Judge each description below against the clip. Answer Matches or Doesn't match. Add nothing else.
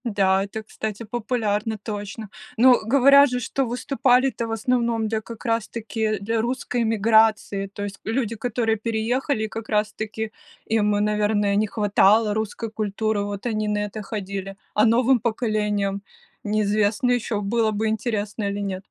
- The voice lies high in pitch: Matches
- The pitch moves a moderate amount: Doesn't match